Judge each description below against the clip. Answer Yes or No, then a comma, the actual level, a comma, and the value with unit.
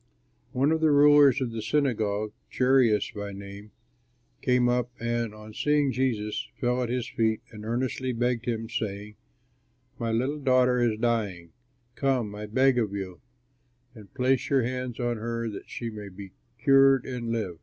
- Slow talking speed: No, average, 165 wpm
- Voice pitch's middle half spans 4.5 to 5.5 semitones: No, average, 3.2 semitones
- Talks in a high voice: No, low, 120 Hz